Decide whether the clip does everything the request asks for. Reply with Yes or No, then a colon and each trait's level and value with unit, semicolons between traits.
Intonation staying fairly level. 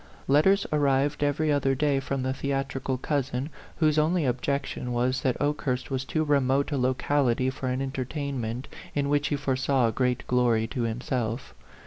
Yes: narrow, 2.2 semitones